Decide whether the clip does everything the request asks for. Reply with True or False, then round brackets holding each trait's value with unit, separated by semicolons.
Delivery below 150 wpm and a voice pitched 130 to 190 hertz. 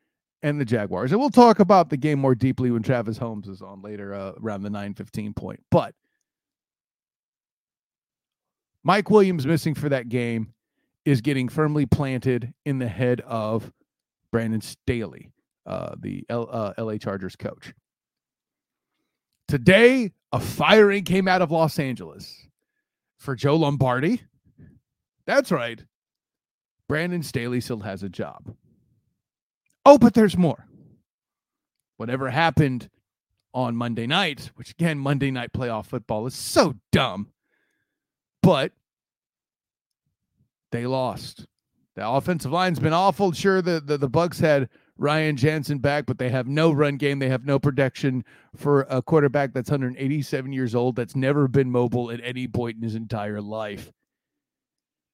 True (140 wpm; 135 Hz)